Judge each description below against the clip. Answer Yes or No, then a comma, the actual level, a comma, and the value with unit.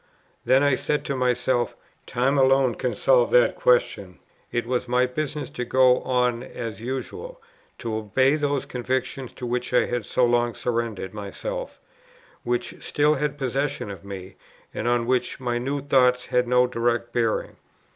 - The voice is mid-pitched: No, low, 125 Hz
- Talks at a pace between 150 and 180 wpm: Yes, average, 160 wpm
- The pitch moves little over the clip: Yes, narrow, 1.9 semitones